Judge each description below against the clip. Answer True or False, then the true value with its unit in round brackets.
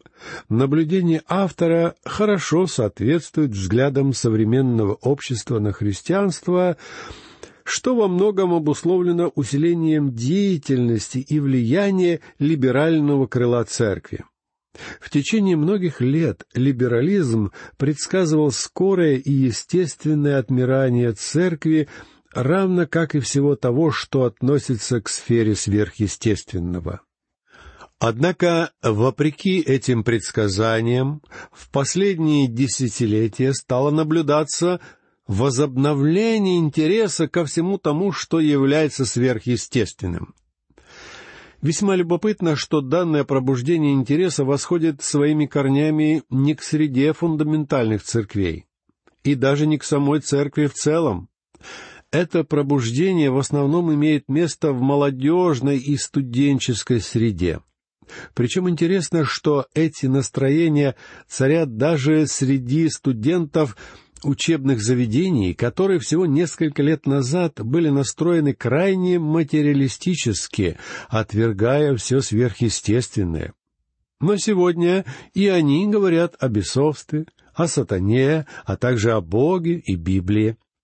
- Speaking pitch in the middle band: True (145 Hz)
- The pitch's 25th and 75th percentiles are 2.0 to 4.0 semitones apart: False (4.7 semitones)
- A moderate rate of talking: False (95 wpm)